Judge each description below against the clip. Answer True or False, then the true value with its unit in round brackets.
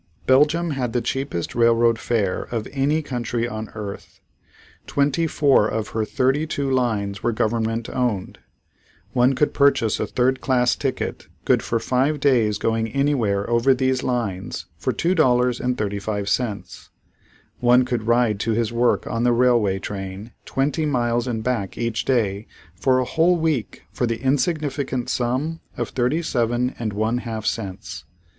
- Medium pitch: False (120 Hz)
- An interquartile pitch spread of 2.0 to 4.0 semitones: True (3.1 semitones)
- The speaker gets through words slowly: False (150 wpm)